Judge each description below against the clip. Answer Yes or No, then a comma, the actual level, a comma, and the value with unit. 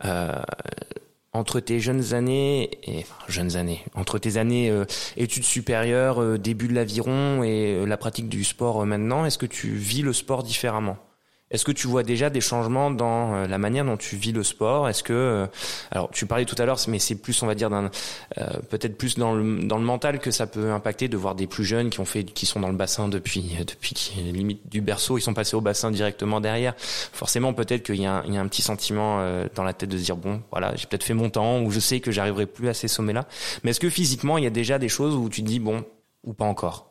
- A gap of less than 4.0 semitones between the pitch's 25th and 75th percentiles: Yes, average, 3.0 semitones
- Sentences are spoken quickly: Yes, fast, 250 wpm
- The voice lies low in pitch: Yes, low, 110 Hz